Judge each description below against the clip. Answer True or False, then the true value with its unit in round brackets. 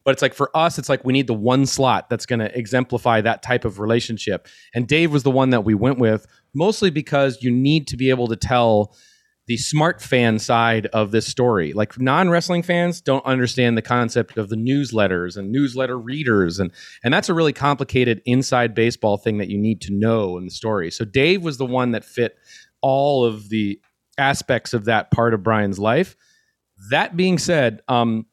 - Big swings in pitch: False (3.6 semitones)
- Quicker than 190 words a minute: True (205 wpm)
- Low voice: True (125 Hz)